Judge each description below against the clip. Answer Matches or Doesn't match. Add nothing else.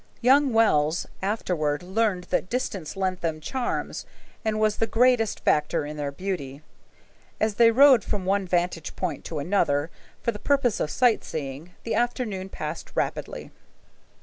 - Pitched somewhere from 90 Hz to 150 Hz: Doesn't match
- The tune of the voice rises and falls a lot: Matches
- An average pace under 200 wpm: Matches